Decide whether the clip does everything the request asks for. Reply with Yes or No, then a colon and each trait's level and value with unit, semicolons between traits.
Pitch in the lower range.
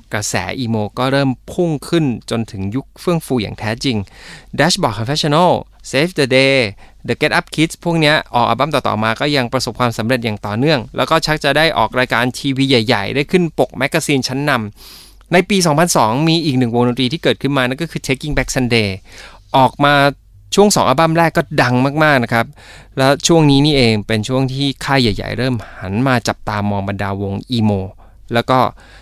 Yes: low, 130 Hz